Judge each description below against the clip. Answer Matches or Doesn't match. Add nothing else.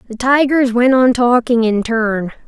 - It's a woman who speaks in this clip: Matches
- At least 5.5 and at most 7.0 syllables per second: Doesn't match